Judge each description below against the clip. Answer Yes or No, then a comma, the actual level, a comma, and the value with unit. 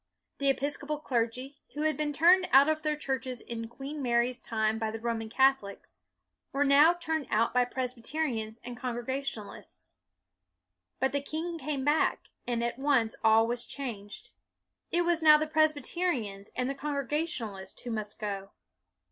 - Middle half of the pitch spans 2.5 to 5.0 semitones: Yes, average, 4.5 semitones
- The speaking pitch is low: No, very high, 265 Hz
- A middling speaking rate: Yes, average, 155 wpm